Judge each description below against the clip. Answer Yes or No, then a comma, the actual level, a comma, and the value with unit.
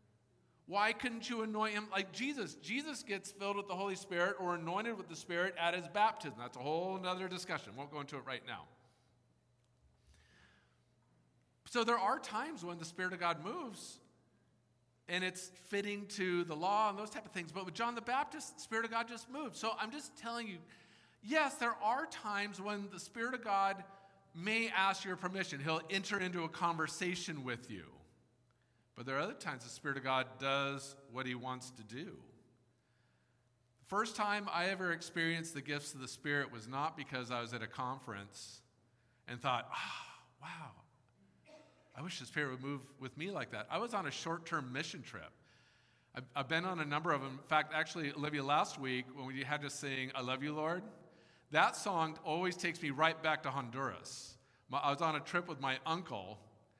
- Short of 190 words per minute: No, average, 195 wpm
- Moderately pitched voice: Yes, medium, 160 Hz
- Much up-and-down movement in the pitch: Yes, wide, 7.0 semitones